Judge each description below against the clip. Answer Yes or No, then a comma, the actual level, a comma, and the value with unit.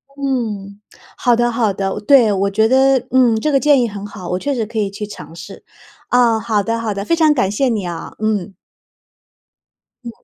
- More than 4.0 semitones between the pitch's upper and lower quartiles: No, average, 3.7 semitones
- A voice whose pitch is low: No, high, 220 Hz